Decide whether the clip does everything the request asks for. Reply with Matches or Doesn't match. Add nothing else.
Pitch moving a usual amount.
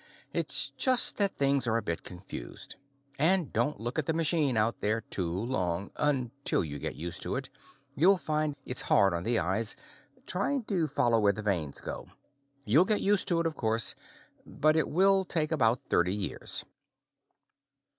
Doesn't match